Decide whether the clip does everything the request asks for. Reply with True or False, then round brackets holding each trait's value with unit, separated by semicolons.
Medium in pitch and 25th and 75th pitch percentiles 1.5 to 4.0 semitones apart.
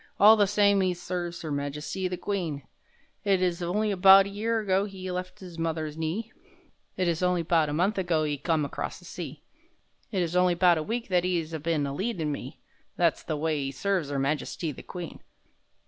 True (175 Hz; 3.5 semitones)